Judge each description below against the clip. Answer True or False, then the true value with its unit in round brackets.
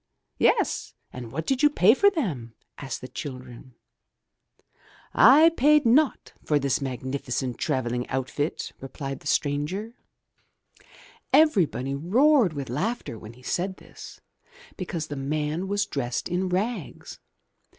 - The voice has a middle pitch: True (150 Hz)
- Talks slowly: True (125 wpm)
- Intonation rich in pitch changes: True (8.5 semitones)